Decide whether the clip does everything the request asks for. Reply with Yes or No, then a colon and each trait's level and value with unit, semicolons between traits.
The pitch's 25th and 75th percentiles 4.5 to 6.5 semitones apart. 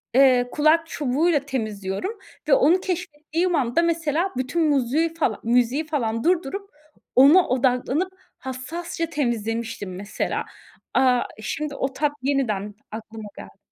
Yes: wide, 5.6 semitones